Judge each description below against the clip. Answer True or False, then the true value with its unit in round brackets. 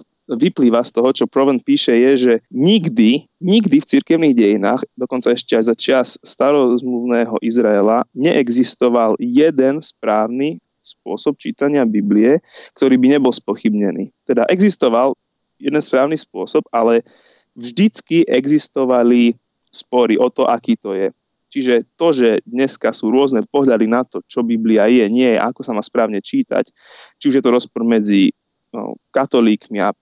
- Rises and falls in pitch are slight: False (4.0 semitones)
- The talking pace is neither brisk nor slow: True (140 wpm)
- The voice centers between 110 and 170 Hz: True (130 Hz)